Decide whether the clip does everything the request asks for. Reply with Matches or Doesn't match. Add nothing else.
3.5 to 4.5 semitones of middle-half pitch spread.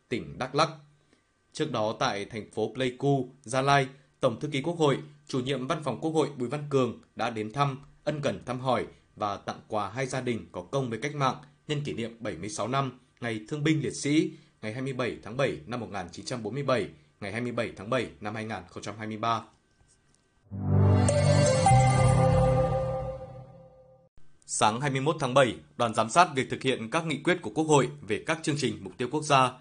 Matches